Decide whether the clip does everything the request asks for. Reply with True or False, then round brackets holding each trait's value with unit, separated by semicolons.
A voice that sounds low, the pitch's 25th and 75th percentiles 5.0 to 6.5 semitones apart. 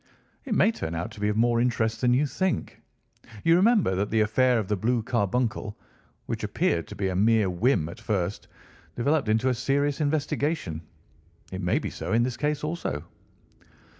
True (115 Hz; 5.5 semitones)